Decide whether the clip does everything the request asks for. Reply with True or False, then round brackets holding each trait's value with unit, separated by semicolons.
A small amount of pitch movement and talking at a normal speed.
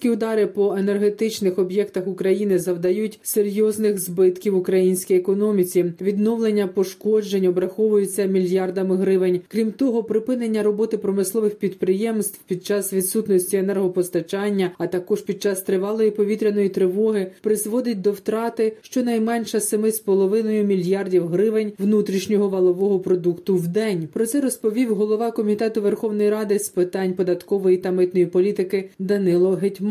True (2.3 semitones; 120 wpm)